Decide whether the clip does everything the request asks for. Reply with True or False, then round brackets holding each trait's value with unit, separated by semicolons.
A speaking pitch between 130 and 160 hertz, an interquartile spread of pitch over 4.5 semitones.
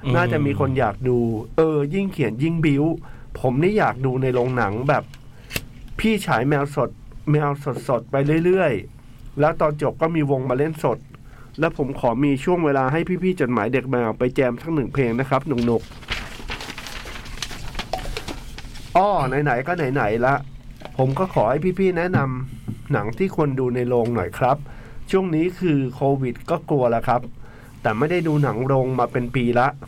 False (135 Hz; 3.8 semitones)